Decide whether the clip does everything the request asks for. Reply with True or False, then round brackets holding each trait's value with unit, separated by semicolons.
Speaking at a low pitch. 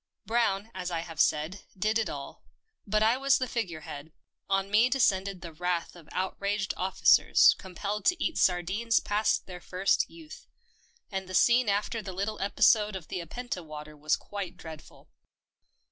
False (195 Hz)